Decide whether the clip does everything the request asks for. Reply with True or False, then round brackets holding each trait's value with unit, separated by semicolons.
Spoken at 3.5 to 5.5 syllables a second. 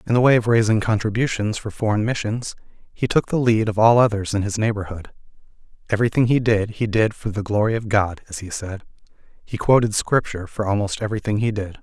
False (6.1 syllables/s)